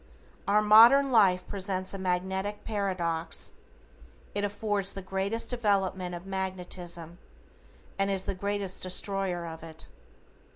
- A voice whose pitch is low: No, high, 190 Hz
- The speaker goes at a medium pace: No, slow, 120 wpm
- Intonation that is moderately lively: No, narrow, 2.0 semitones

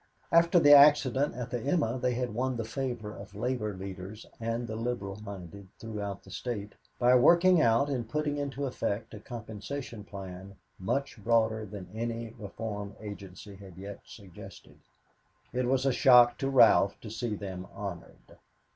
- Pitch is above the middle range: No, low, 115 Hz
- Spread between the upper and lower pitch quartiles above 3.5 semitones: Yes, average, 4.0 semitones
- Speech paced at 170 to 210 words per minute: No, average, 160 wpm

